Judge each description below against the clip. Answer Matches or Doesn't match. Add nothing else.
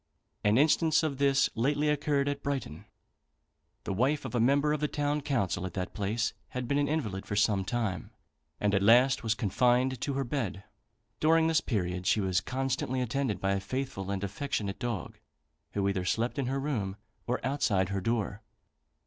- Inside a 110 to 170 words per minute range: Doesn't match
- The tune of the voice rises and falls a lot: Matches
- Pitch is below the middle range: Matches